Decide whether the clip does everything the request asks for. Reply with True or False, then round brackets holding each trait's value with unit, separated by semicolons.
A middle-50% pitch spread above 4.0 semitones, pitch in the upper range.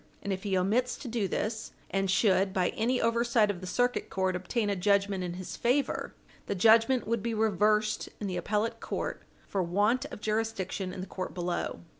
False (3.2 semitones; 205 Hz)